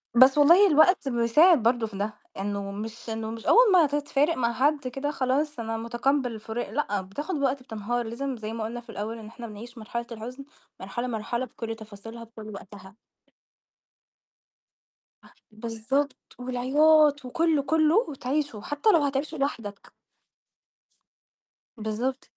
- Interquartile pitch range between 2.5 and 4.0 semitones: No, average, 4.5 semitones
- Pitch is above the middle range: Yes, high, 245 Hz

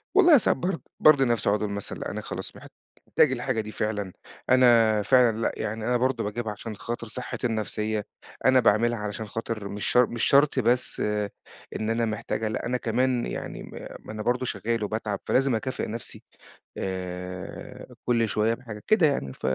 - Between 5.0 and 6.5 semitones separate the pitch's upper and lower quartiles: No, average, 2.7 semitones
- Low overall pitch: Yes, low, 115 Hz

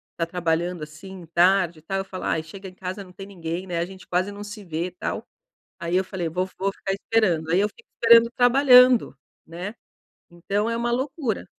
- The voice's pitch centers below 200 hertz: Yes, high, 190 Hz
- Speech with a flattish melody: No, average, 3.3 semitones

